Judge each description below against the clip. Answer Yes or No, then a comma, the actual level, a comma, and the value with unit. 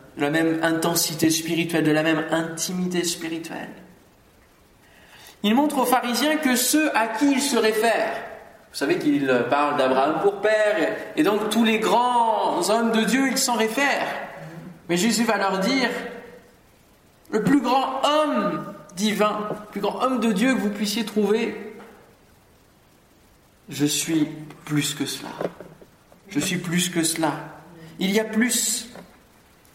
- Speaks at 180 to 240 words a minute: No, slow, 145 wpm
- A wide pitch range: Yes, wide, 6.1 semitones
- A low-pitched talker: No, high, 210 Hz